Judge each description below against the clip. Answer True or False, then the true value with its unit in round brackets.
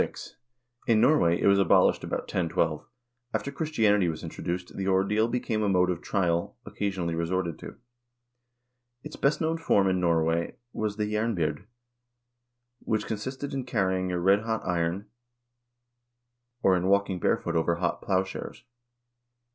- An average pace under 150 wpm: True (140 wpm)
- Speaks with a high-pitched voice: False (95 Hz)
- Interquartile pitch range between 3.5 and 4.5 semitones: True (3.8 semitones)